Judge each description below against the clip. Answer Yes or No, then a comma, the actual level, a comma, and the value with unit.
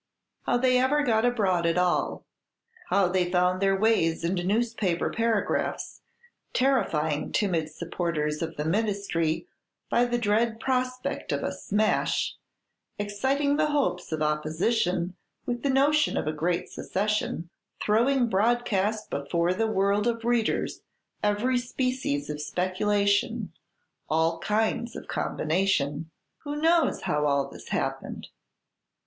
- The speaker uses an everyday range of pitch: No, wide, 6.1 semitones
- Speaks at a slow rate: Yes, slow, 125 wpm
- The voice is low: No, high, 205 Hz